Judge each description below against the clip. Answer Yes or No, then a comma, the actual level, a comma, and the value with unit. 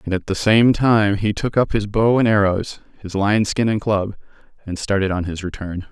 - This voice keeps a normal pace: No, fast, 225 wpm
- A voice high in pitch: No, low, 100 Hz